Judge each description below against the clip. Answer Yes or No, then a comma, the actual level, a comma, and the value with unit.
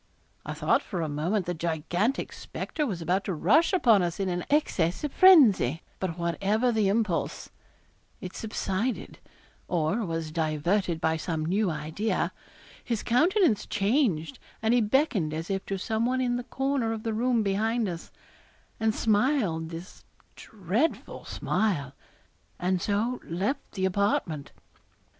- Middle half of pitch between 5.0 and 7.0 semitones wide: Yes, wide, 5.5 semitones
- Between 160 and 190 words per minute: No, average, 145 wpm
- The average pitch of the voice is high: Yes, high, 200 Hz